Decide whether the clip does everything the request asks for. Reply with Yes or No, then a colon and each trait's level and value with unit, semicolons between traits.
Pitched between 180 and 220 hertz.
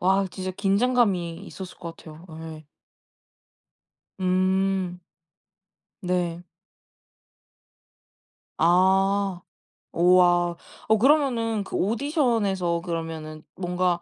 Yes: medium, 185 Hz